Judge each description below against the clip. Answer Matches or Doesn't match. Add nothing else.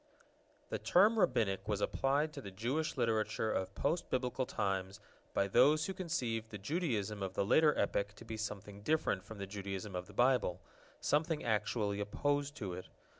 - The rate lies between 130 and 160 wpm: Doesn't match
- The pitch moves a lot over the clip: Matches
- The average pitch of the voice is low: Matches